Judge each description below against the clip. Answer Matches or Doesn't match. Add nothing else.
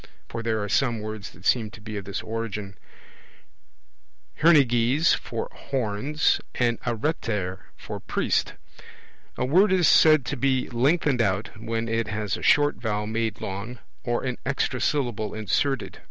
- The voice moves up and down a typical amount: Matches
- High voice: Doesn't match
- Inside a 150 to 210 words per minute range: Matches